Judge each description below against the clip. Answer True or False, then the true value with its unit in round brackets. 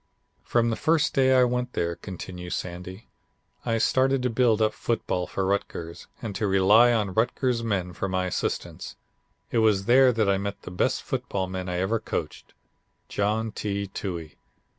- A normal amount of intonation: True (4.1 semitones)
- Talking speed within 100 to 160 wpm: False (170 wpm)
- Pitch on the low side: True (105 Hz)